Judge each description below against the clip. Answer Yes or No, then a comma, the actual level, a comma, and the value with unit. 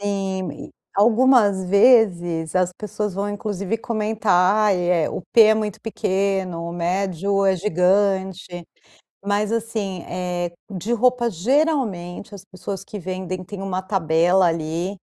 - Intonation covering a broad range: No, average, 2.7 semitones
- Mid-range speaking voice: No, high, 195 Hz